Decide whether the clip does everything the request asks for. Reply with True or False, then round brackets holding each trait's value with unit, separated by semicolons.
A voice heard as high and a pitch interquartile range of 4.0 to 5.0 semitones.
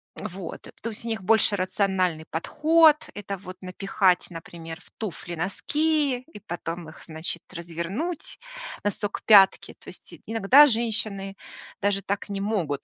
True (195 Hz; 4.3 semitones)